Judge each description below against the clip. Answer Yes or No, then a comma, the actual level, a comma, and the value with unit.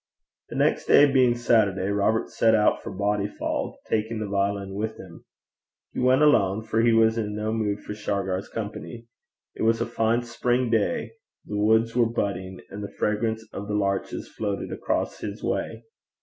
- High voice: No, low, 110 Hz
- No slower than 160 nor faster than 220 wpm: Yes, average, 175 wpm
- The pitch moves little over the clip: Yes, narrow, 2.1 semitones